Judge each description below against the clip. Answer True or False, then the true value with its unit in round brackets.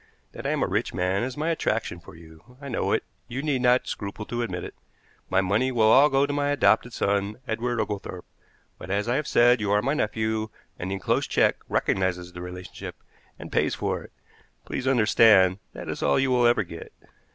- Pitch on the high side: False (110 Hz)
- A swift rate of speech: True (215 wpm)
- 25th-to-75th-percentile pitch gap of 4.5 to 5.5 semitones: True (4.8 semitones)